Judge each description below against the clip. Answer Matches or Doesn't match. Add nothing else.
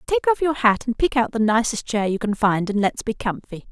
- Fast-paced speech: Matches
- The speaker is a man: Doesn't match